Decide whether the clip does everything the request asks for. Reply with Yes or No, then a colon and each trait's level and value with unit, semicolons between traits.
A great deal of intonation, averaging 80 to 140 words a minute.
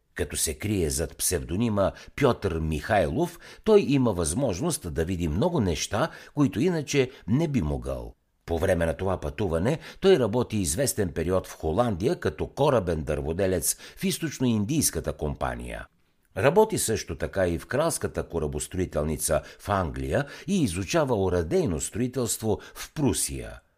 Yes: wide, 7.0 semitones; average, 130 wpm